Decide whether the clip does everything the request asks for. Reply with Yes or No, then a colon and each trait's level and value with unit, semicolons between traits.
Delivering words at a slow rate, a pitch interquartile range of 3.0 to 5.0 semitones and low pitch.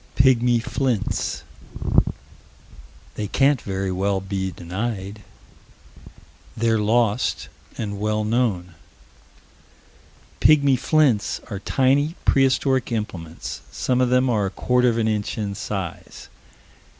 Yes: slow, 105 wpm; average, 4.2 semitones; low, 110 Hz